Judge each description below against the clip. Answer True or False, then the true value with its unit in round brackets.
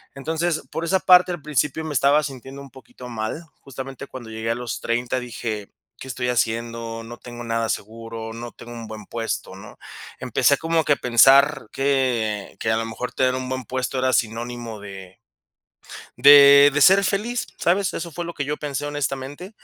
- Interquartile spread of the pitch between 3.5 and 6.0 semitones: True (4.0 semitones)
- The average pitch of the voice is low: True (130 Hz)